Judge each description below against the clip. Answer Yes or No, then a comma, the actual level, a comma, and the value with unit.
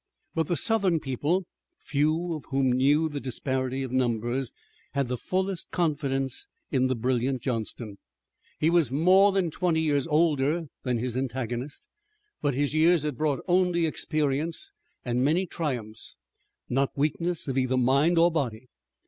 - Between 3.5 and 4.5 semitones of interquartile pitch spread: Yes, average, 4.1 semitones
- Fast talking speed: No, average, 150 wpm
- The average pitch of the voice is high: No, medium, 140 Hz